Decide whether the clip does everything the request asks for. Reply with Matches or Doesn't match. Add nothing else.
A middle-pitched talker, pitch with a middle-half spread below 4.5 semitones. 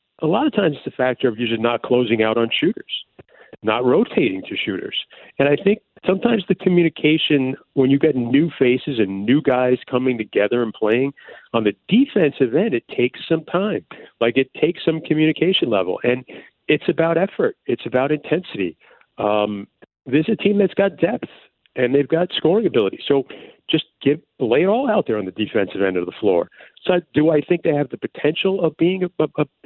Doesn't match